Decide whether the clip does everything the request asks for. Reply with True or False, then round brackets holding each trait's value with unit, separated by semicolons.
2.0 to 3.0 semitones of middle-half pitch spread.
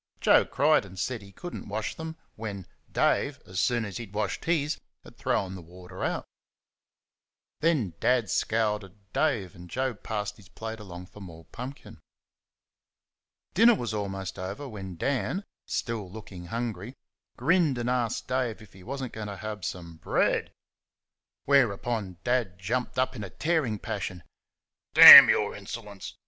False (4.8 semitones)